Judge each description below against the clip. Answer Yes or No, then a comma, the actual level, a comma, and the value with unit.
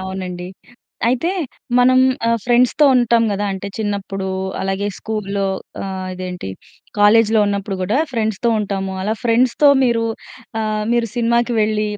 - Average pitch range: Yes, average, 3.3 semitones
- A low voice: No, high, 215 Hz